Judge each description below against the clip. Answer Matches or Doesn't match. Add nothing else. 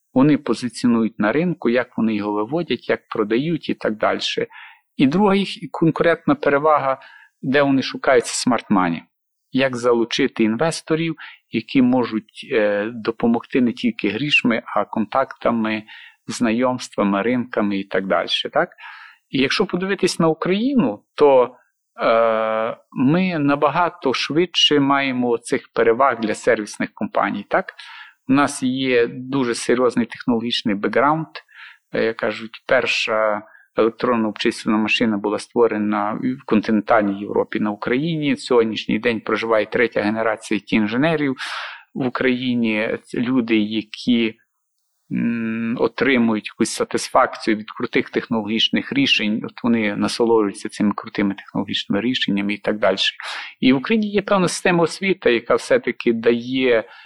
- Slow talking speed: Matches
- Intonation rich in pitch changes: Matches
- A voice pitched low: Matches